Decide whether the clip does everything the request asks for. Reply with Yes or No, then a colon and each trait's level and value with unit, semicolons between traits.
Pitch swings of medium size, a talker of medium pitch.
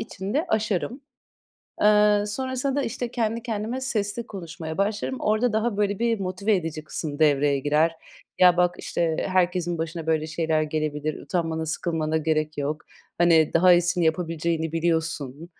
Yes: average, 4.8 semitones; medium, 175 Hz